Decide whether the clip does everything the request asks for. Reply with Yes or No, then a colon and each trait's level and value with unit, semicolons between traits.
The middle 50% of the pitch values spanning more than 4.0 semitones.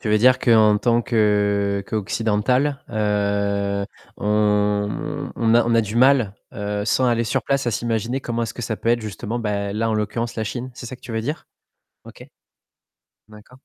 No: narrow, 2.5 semitones